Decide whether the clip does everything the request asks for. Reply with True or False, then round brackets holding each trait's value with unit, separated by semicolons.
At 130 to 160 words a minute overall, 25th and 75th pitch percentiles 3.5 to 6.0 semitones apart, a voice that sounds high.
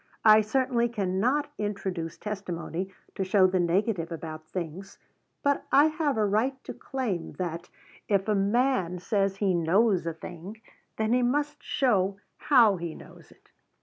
True (150 wpm; 4.9 semitones; 200 Hz)